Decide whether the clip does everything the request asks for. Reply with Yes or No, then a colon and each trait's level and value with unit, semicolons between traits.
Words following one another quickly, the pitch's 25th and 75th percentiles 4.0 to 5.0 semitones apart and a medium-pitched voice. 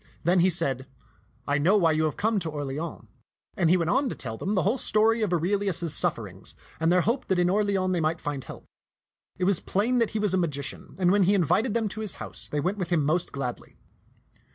Yes: fast, 240 wpm; average, 4.6 semitones; medium, 180 Hz